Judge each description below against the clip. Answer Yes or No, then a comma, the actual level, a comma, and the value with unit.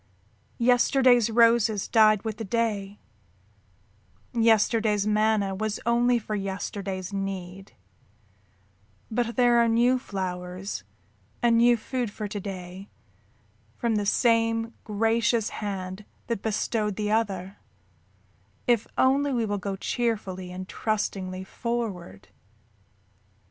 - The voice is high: Yes, high, 215 Hz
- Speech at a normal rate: No, slow, 105 wpm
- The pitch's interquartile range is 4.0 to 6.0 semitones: No, average, 3.1 semitones